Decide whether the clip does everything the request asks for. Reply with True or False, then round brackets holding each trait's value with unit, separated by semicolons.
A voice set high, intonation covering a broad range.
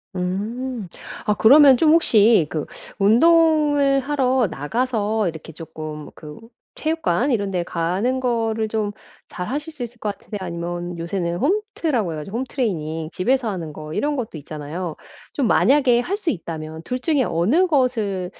True (220 Hz; 7.5 semitones)